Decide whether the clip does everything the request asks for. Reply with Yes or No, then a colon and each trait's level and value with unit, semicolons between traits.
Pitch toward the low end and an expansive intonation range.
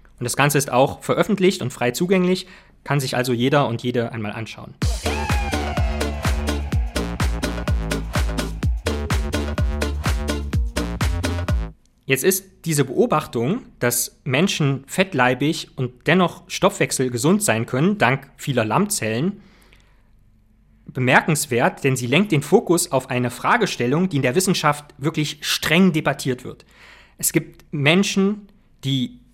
Yes: low, 130 Hz; wide, 7.4 semitones